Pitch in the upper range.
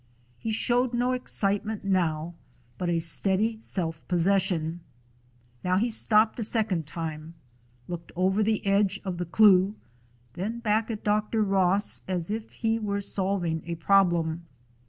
Yes: high, 195 Hz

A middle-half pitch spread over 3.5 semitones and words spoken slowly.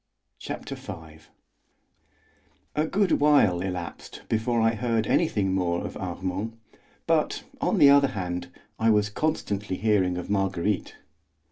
Yes: average, 4.0 semitones; slow, 125 wpm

